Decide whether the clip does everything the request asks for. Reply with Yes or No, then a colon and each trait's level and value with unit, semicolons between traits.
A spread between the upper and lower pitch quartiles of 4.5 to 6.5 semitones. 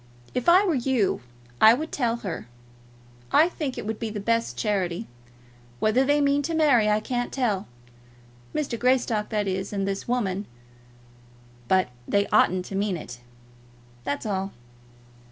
Yes: average, 4.9 semitones